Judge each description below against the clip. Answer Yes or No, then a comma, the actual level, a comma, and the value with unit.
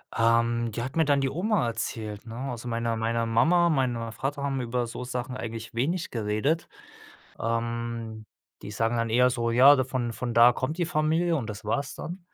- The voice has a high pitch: No, low, 120 Hz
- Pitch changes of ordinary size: Yes, average, 3.3 semitones